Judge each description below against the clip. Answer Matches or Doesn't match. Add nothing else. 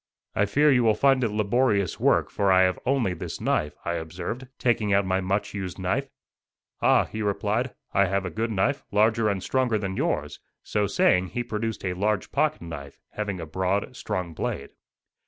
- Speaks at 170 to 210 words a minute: Matches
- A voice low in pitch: Matches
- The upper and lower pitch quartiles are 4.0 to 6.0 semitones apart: Doesn't match